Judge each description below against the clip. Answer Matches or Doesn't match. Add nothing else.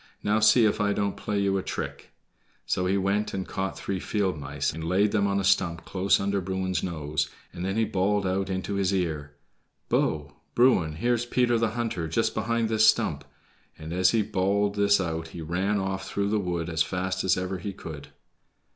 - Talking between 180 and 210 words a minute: Matches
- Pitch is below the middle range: Matches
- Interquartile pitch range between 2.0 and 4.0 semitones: Matches